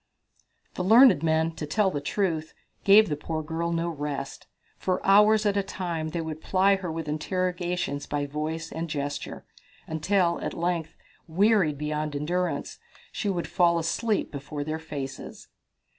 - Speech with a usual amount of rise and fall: Yes, average, 3.5 semitones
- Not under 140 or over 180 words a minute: Yes, average, 160 wpm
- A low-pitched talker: No, medium, 165 Hz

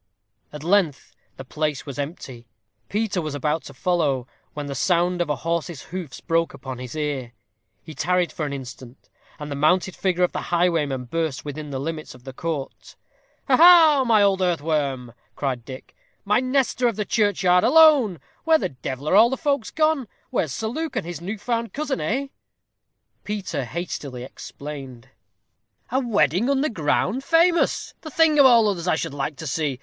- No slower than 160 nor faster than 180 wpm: Yes, average, 175 wpm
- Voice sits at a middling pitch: Yes, medium, 170 Hz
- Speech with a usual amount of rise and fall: No, wide, 7.8 semitones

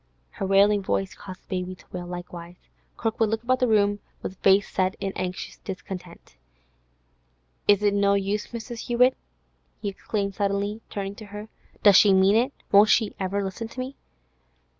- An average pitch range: No, narrow, 2.2 semitones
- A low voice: No, high, 200 Hz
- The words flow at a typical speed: Yes, average, 170 wpm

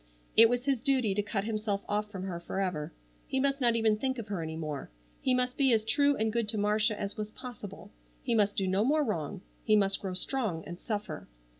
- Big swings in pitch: No, average, 3.8 semitones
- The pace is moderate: No, fast, 230 wpm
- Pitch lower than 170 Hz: No, high, 215 Hz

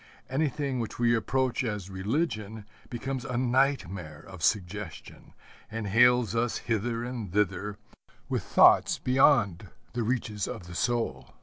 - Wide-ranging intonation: No, average, 4.0 semitones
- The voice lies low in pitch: Yes, low, 115 Hz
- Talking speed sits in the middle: No, slow, 130 wpm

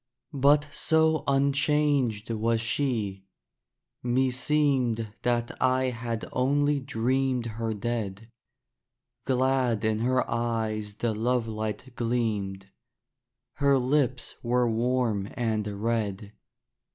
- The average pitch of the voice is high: No, low, 120 Hz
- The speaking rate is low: Yes, slow, 90 wpm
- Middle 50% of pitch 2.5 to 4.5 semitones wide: Yes, average, 3.0 semitones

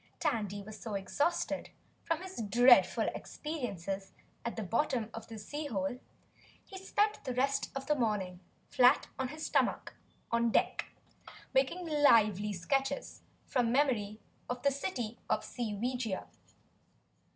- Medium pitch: No, high, 245 Hz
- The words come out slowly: Yes, slow, 130 wpm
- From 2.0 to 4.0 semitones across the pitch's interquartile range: No, average, 4.9 semitones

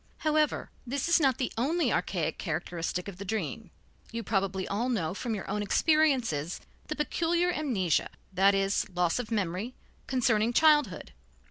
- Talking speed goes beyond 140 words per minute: Yes, average, 150 wpm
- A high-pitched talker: Yes, high, 220 Hz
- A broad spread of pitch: Yes, wide, 6.8 semitones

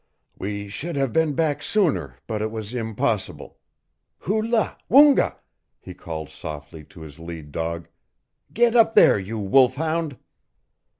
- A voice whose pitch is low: Yes, low, 110 Hz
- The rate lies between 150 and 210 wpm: No, average, 140 wpm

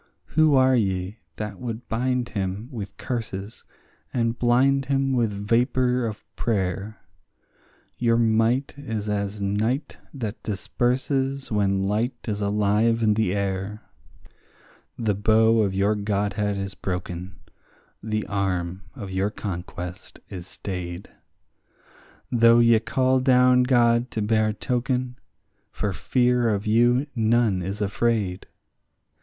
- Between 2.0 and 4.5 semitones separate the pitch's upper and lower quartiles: Yes, average, 3.5 semitones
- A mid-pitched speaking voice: No, low, 110 Hz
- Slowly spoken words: Yes, slow, 120 wpm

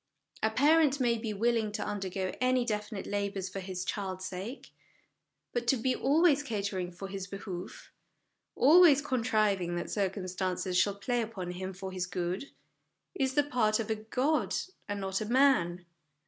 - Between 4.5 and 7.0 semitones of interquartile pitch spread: Yes, average, 5.0 semitones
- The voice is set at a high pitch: Yes, high, 210 Hz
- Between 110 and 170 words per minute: Yes, average, 160 wpm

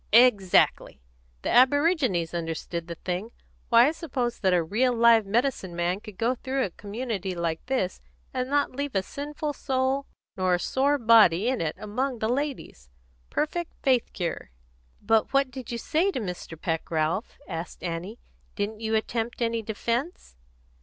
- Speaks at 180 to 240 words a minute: No, average, 160 wpm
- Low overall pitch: No, high, 225 Hz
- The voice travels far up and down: Yes, wide, 6.1 semitones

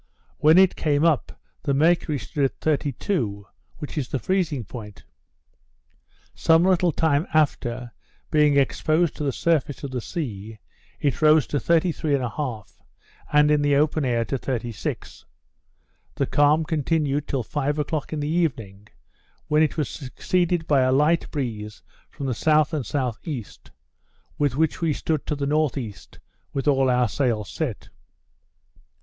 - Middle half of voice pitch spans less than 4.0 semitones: Yes, average, 3.5 semitones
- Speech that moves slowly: No, average, 150 wpm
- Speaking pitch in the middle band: Yes, medium, 145 Hz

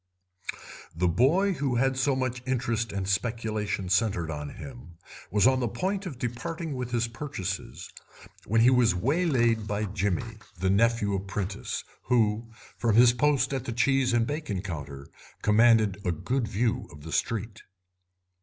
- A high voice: No, low, 115 Hz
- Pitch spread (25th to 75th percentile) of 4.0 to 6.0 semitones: Yes, average, 4.4 semitones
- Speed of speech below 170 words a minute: Yes, average, 155 wpm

